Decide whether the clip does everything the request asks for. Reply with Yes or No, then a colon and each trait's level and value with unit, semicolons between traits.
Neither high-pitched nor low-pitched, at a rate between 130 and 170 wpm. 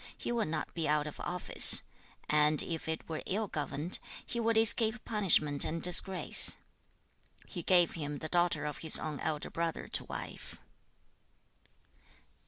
Yes: medium, 165 Hz; average, 150 wpm